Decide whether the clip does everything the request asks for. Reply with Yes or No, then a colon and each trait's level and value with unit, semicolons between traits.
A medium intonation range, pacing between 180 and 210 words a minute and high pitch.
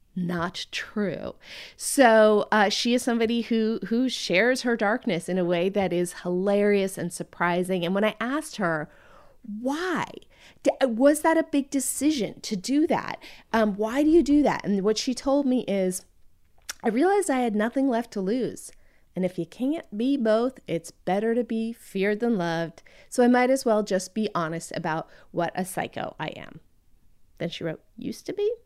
No: wide, 5.8 semitones; average, 185 wpm; high, 220 Hz